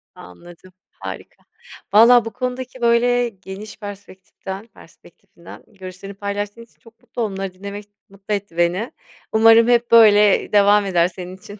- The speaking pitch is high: Yes, high, 205 Hz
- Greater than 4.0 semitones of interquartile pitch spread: No, average, 3.2 semitones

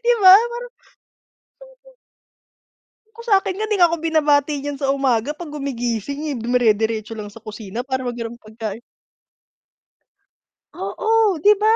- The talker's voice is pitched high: Yes, very high, 280 Hz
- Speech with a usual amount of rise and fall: No, wide, 8.3 semitones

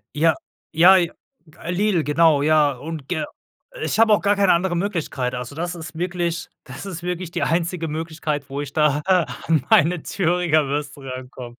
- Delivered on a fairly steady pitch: No, average, 3.2 semitones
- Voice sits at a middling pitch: Yes, medium, 165 Hz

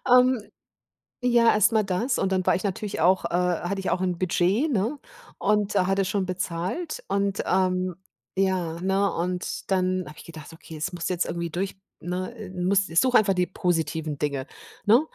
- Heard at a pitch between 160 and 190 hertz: Yes, medium, 185 Hz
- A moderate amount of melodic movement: No, narrow, 2.3 semitones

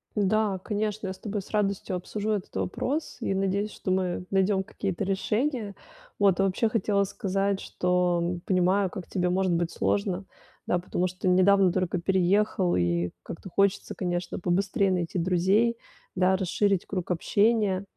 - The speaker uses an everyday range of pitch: No, narrow, 2.0 semitones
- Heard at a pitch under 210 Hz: Yes, high, 190 Hz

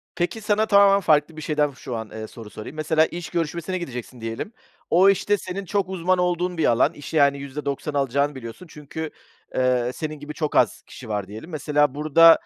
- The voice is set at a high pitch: No, medium, 150 Hz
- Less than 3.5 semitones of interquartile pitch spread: No, average, 5.0 semitones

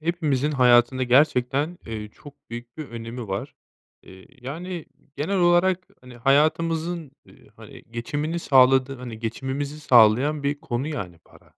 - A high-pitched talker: No, low, 135 Hz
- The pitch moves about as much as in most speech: Yes, average, 4.4 semitones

